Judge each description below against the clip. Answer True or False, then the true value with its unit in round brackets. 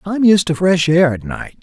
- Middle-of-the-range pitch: True (180 Hz)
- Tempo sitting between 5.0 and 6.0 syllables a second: False (4.7 syllables/s)